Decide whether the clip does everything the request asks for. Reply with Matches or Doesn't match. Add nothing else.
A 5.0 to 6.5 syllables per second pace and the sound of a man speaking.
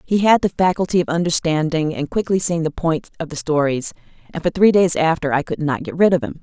Doesn't match